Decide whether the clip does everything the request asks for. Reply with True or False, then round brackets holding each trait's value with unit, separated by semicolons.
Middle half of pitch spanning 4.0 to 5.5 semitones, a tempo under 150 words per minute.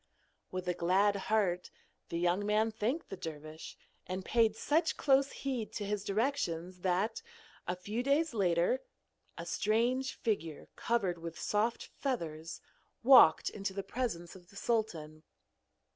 True (5.1 semitones; 140 wpm)